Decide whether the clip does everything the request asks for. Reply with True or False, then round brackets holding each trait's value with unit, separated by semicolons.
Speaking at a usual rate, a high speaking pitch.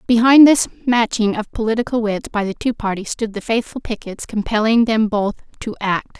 True (185 wpm; 225 Hz)